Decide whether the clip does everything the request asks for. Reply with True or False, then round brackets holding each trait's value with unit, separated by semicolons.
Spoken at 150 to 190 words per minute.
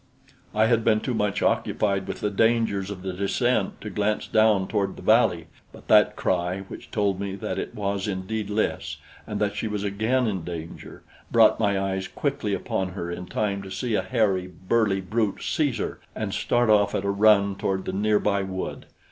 False (200 wpm)